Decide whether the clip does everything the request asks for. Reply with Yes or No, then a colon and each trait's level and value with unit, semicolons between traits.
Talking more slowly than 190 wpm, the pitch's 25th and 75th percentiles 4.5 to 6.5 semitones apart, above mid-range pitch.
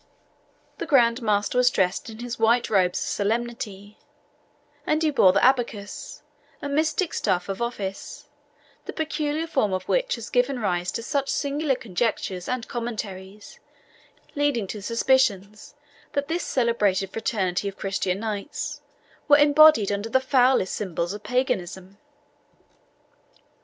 Yes: slow, 135 wpm; average, 5.2 semitones; high, 230 Hz